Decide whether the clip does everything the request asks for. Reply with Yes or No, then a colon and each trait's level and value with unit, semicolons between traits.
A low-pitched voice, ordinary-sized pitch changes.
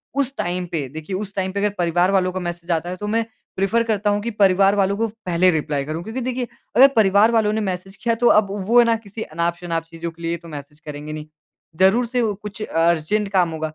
No: high, 190 Hz; average, 4.1 semitones